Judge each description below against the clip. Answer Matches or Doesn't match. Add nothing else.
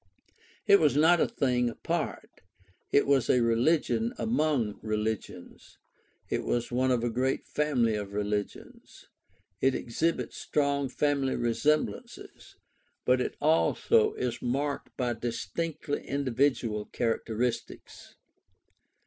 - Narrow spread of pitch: Doesn't match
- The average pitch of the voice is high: Doesn't match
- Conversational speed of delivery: Doesn't match